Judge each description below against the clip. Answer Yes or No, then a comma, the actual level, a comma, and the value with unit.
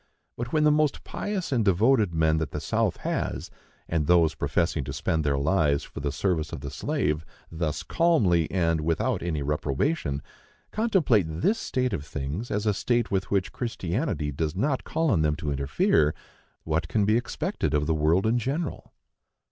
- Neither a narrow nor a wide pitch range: No, wide, 7.8 semitones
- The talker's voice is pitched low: Yes, very low, 85 Hz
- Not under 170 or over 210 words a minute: Yes, average, 180 wpm